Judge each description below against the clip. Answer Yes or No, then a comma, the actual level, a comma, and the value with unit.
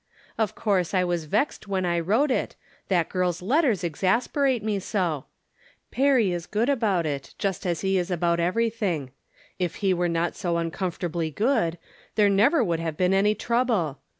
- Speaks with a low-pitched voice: No, medium, 185 Hz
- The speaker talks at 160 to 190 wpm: Yes, average, 170 wpm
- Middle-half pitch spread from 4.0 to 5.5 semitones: Yes, average, 4.3 semitones